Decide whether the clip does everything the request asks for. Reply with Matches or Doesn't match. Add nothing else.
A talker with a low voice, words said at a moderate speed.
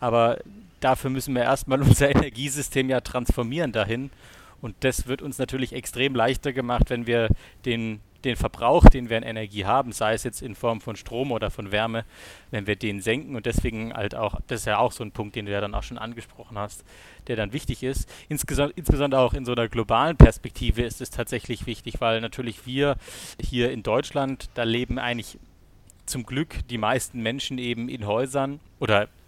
Doesn't match